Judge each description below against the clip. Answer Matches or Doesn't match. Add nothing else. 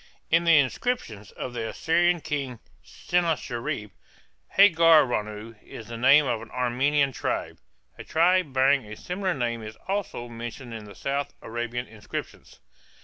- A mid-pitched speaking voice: Doesn't match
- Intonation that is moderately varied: Doesn't match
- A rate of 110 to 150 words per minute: Matches